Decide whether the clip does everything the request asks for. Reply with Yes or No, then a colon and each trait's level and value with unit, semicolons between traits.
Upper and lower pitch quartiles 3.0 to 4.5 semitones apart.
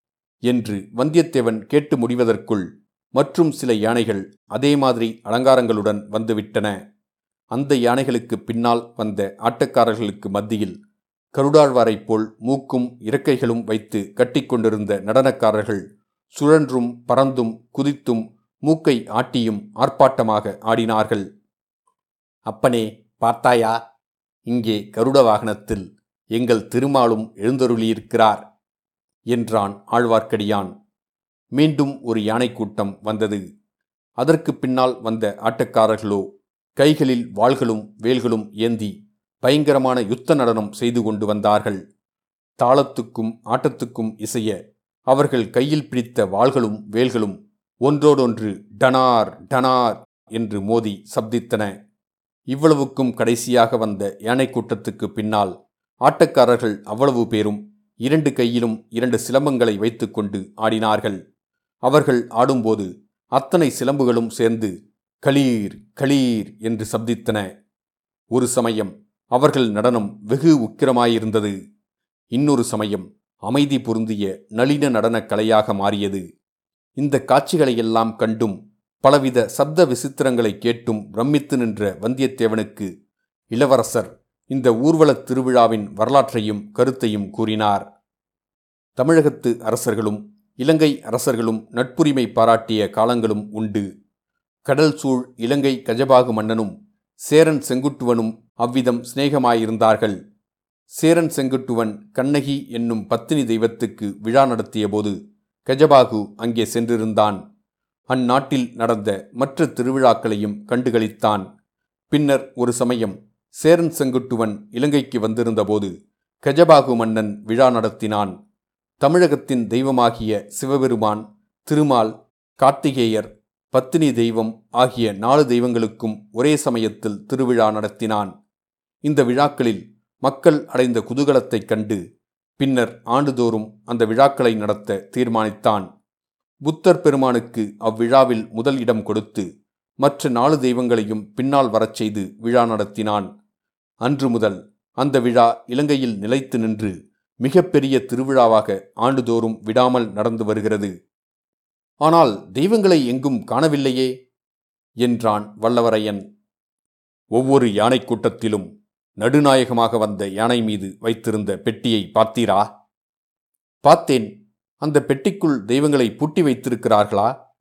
Yes: average, 3.5 semitones